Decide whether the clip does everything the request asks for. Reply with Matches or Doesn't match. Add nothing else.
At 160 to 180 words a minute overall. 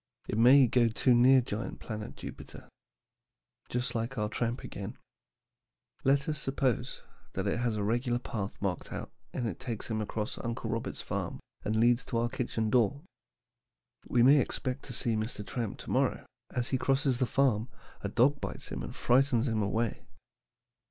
Matches